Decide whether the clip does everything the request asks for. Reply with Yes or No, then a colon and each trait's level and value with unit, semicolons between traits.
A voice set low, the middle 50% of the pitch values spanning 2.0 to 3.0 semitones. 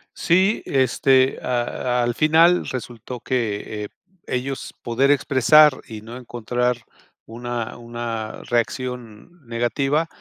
Yes: low, 125 Hz; narrow, 2.6 semitones